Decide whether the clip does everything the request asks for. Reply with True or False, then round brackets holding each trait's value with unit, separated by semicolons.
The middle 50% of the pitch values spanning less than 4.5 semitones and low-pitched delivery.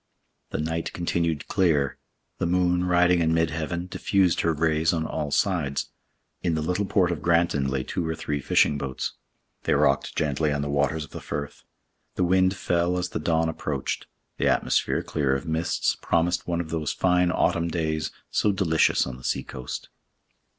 True (3.0 semitones; 80 Hz)